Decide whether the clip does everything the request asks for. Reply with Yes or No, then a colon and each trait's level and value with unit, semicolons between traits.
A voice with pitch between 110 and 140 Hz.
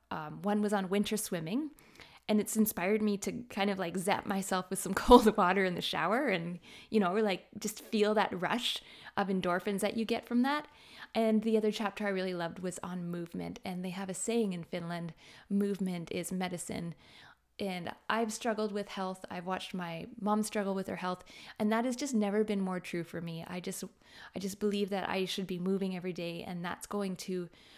No: high, 195 Hz